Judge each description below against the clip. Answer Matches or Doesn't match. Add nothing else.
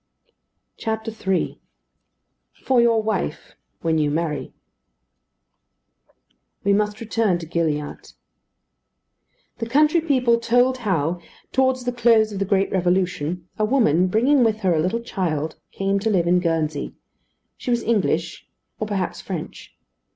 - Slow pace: Matches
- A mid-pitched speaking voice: Doesn't match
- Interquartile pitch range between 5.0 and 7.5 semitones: Matches